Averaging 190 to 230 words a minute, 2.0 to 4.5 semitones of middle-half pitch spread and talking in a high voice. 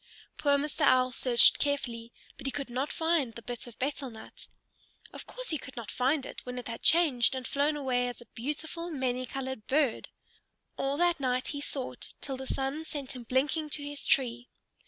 Yes: average, 200 wpm; average, 2.7 semitones; very high, 265 Hz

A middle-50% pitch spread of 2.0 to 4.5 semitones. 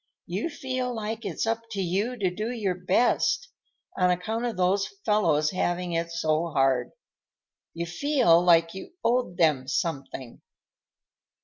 No: average, 5.2 semitones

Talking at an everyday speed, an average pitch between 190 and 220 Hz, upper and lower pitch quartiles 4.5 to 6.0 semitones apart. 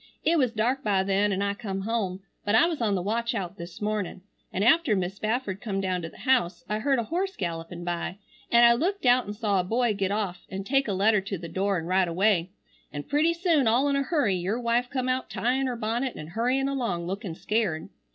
No: fast, 235 wpm; high, 215 Hz; average, 4.8 semitones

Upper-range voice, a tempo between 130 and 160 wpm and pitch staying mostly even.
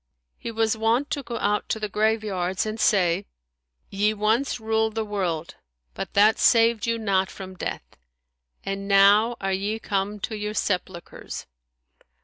Yes: high, 210 Hz; average, 150 wpm; narrow, 2.1 semitones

